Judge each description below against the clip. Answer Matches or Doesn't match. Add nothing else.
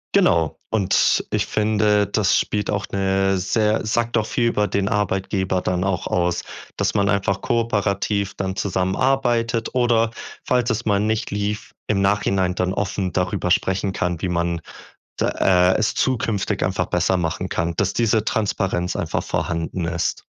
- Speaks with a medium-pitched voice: Doesn't match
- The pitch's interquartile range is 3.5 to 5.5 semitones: Doesn't match